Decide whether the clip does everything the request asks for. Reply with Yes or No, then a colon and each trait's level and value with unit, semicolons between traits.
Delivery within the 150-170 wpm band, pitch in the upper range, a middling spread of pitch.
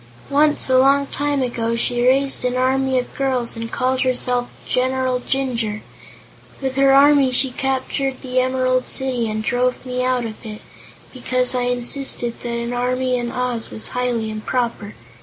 No: average, 160 wpm; very high, 255 Hz; narrow, 1.5 semitones